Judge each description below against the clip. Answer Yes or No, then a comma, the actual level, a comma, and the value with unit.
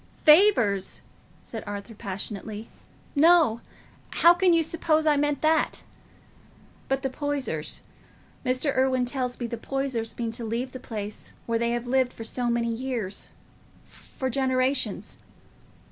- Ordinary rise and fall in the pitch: Yes, average, 3.7 semitones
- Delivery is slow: Yes, slow, 125 wpm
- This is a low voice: No, very high, 255 Hz